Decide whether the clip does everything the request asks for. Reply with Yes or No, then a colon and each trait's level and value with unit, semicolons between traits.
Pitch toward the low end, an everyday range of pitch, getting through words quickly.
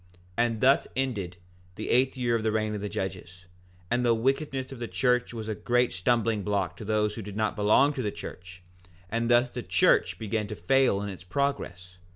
Yes: low, 110 Hz; average, 3.5 semitones; fast, 210 wpm